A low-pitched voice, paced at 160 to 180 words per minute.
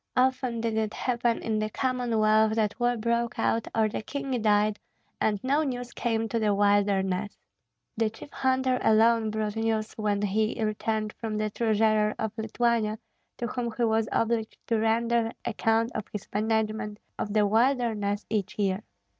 No: high, 220 Hz; average, 165 wpm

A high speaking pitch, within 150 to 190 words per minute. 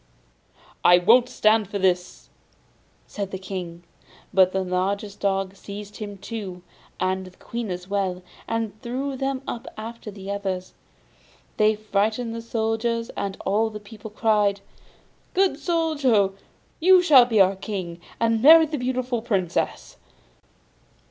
No: high, 210 Hz; slow, 135 wpm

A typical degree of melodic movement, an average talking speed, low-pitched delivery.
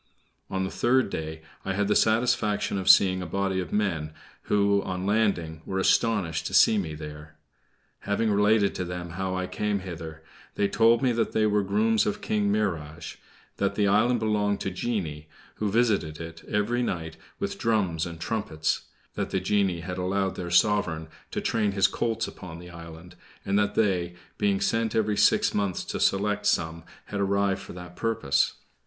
Yes: average, 3.4 semitones; average, 175 wpm; low, 100 Hz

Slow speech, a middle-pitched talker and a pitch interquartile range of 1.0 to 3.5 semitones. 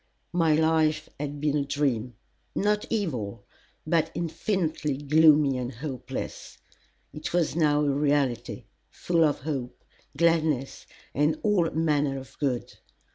Yes: slow, 125 wpm; medium, 150 Hz; average, 2.8 semitones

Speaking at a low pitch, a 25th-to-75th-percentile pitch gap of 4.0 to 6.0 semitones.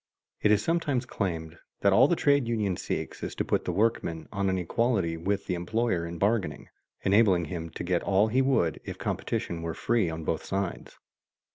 Yes: low, 100 Hz; average, 5.3 semitones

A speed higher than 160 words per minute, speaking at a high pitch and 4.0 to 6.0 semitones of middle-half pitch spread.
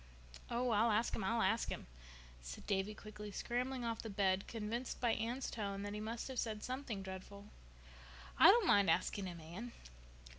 No: average, 170 wpm; high, 215 Hz; average, 3.0 semitones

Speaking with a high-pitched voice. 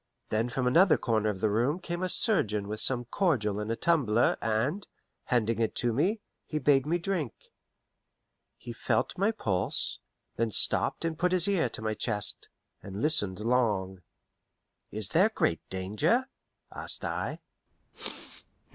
No: low, 120 Hz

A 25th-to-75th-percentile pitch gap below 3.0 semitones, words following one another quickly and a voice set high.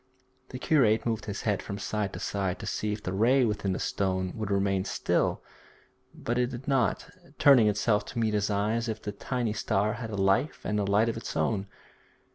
No: narrow, 2.5 semitones; fast, 215 wpm; low, 105 Hz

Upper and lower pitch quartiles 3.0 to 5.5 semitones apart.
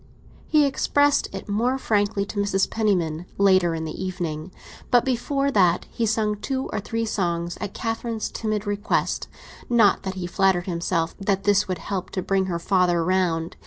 Yes: average, 3.7 semitones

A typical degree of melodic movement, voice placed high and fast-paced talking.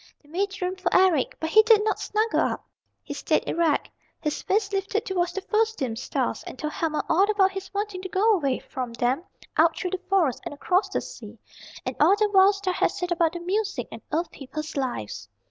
Yes: average, 4.3 semitones; very high, 370 Hz; fast, 215 wpm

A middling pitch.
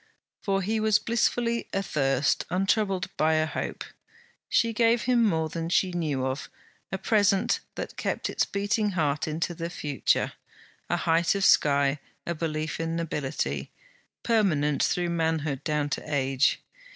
Yes: medium, 165 Hz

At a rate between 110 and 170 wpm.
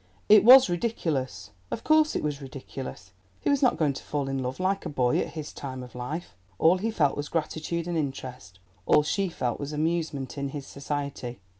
No: average, 190 wpm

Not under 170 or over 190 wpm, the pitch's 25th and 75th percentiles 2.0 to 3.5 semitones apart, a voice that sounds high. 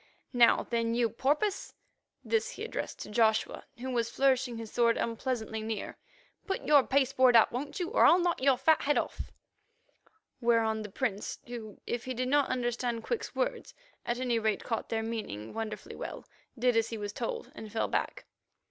Yes: average, 175 wpm; average, 3.0 semitones; high, 240 Hz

